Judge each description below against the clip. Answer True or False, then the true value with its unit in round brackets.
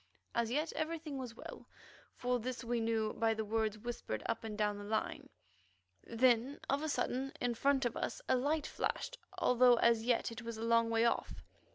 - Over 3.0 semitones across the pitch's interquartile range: False (2.4 semitones)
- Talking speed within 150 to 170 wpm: False (195 wpm)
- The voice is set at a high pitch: True (235 Hz)